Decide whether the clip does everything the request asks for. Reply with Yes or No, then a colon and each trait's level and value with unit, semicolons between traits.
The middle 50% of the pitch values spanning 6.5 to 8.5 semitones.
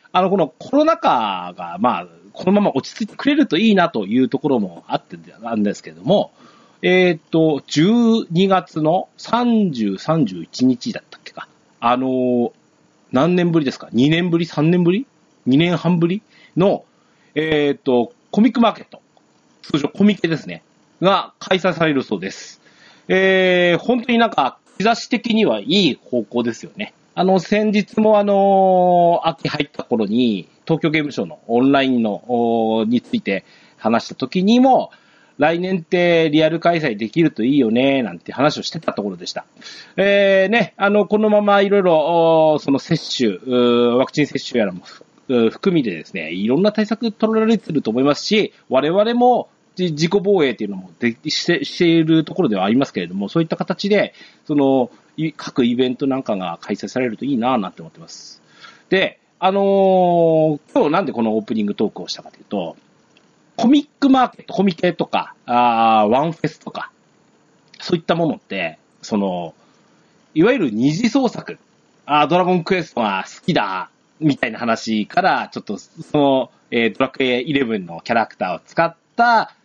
Yes: wide, 7.2 semitones